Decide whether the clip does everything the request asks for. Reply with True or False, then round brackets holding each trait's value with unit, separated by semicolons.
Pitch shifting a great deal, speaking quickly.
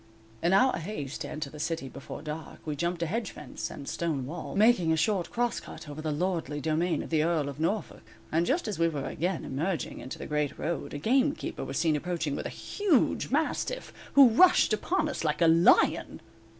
True (5.7 semitones; 210 wpm)